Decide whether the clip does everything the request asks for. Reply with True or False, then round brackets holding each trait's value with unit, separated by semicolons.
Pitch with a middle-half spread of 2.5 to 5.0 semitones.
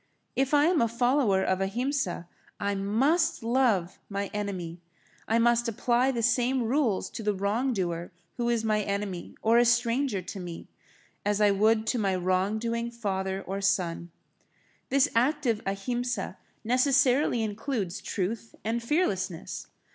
True (4.1 semitones)